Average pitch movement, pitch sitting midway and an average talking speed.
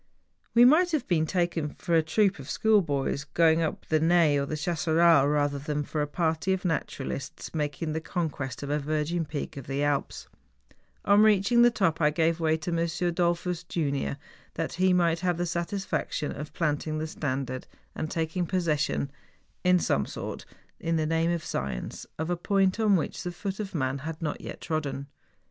Yes: average, 3.1 semitones; medium, 160 Hz; average, 190 wpm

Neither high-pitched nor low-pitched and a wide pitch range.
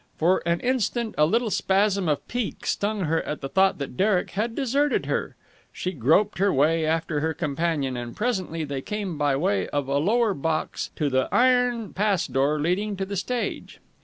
Yes: medium, 180 Hz; wide, 5.9 semitones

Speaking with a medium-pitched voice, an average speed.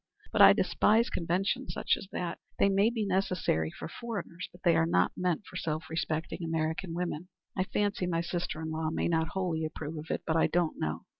No: medium, 170 Hz; fast, 210 wpm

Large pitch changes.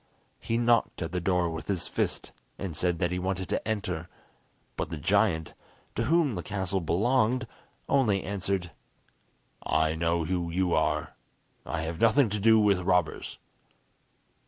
No: average, 3.9 semitones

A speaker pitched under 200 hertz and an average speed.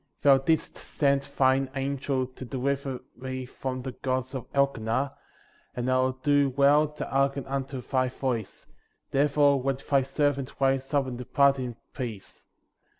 Yes: low, 135 Hz; average, 150 wpm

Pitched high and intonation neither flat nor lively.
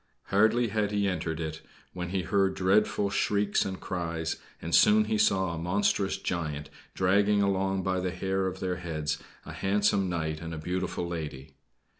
No: very low, 95 Hz; average, 3.0 semitones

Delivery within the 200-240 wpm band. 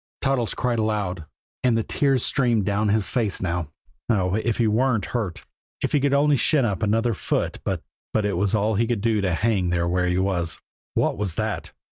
Yes: fast, 205 wpm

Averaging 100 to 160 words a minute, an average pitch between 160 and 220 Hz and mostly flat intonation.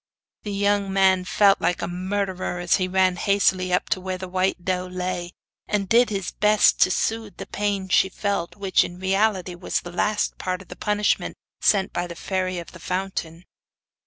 No: average, 190 wpm; high, 190 Hz; narrow, 1.8 semitones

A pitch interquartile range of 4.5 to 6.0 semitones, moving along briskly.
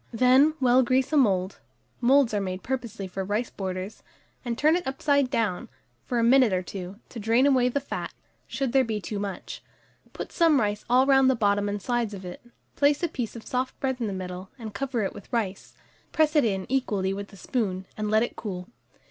Yes: average, 4.8 semitones; fast, 215 wpm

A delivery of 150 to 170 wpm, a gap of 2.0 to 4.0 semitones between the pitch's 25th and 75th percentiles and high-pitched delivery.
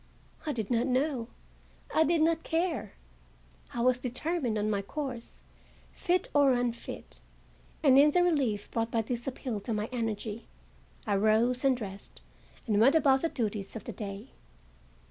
No: average, 160 wpm; average, 4.7 semitones; high, 245 Hz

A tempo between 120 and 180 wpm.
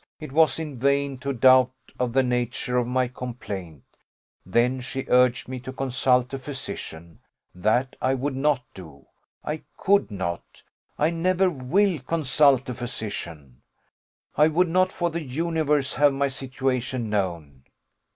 Yes: average, 145 wpm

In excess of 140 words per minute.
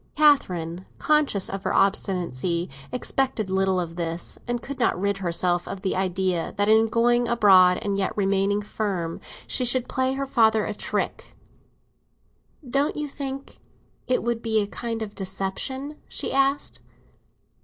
Yes: average, 150 wpm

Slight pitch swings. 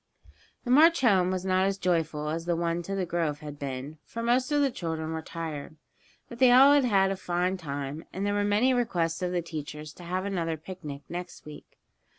No: average, 4.2 semitones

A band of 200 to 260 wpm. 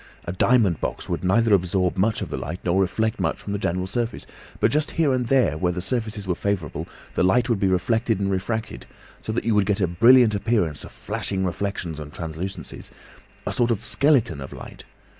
Yes: fast, 205 wpm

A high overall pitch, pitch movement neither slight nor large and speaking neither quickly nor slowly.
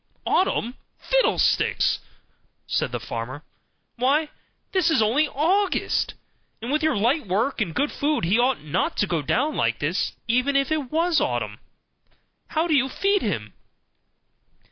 No: very high, 265 Hz; wide, 7.1 semitones; average, 145 wpm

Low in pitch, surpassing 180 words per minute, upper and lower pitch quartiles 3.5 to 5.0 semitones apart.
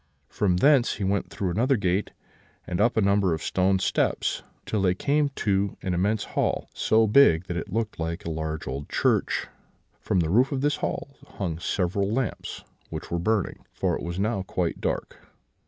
Yes: low, 100 Hz; average, 190 wpm; average, 3.9 semitones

